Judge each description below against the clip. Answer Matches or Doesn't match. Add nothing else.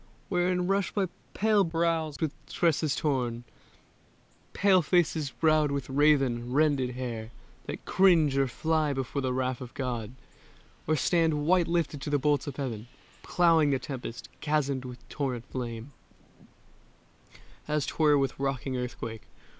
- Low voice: Doesn't match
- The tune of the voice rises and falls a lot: Doesn't match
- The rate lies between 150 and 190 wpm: Doesn't match